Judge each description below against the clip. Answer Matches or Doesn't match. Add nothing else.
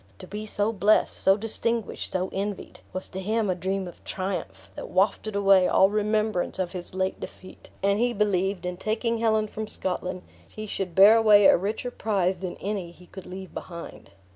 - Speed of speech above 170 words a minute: Matches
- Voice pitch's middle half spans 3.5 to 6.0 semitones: Doesn't match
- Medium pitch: Doesn't match